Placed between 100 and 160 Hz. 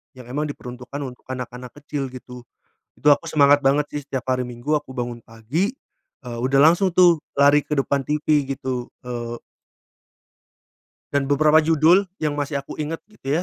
Yes: medium, 140 Hz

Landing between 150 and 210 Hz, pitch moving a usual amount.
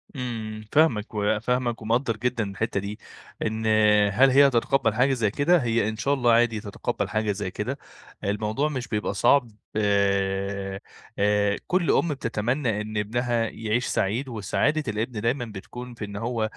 No: low, 110 Hz; average, 3.0 semitones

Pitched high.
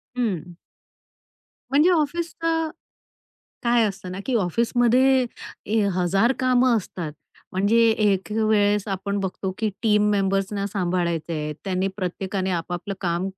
Yes: high, 200 Hz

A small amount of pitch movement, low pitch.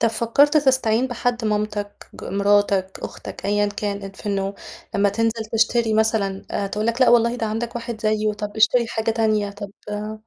No: narrow, 2.0 semitones; high, 215 Hz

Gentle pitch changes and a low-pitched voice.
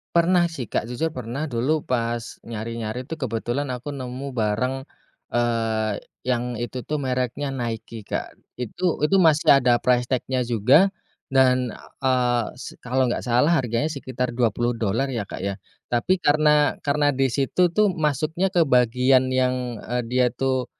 No: average, 3.2 semitones; low, 125 Hz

